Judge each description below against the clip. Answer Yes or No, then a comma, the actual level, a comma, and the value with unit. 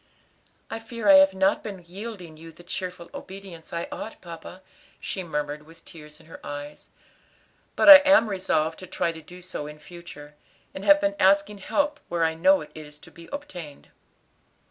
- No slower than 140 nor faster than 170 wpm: No, average, 185 wpm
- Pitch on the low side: No, medium, 180 Hz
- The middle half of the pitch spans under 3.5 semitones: No, average, 3.8 semitones